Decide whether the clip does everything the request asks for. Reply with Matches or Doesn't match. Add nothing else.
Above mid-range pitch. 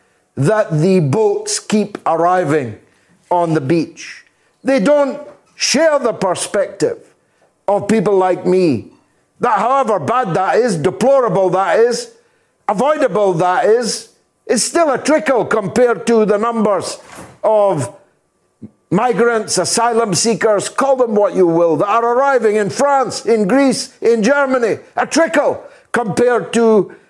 Matches